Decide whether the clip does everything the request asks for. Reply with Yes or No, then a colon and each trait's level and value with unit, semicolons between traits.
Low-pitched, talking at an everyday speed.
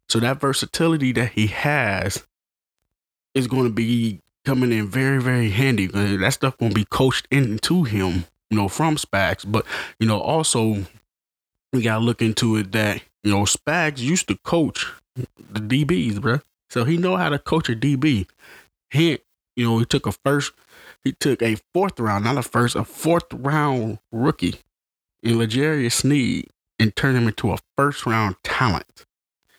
Yes: low, 115 Hz; average, 170 wpm